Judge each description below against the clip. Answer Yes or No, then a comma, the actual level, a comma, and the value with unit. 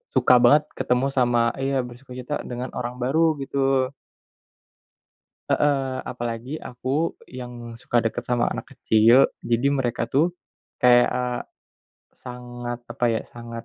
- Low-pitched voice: Yes, low, 125 Hz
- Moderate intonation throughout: No, narrow, 1.8 semitones